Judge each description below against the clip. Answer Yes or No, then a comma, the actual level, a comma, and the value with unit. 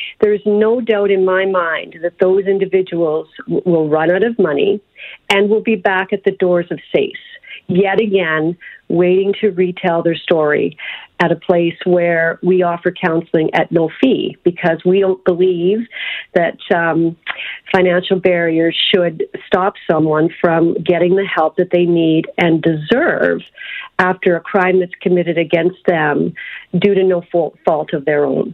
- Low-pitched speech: No, medium, 180 Hz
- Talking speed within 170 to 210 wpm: No, average, 160 wpm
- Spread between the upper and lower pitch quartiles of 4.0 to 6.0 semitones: No, narrow, 2.6 semitones